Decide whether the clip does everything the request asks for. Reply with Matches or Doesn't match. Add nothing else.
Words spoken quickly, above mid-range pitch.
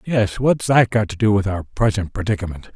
Doesn't match